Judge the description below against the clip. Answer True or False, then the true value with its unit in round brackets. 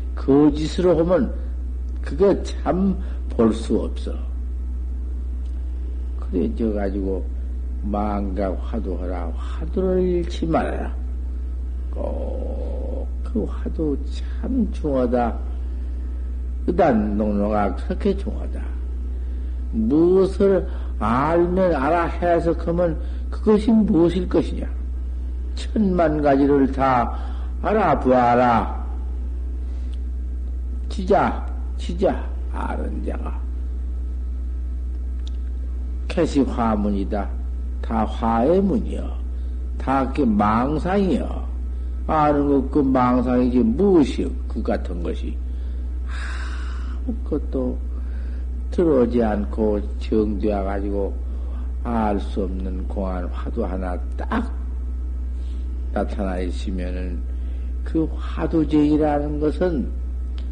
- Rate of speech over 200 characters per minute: False (170 characters per minute)